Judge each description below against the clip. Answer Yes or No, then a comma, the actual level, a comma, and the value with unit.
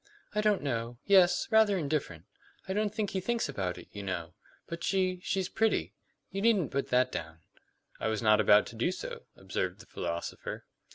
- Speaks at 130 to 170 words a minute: No, average, 185 wpm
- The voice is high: No, medium, 155 Hz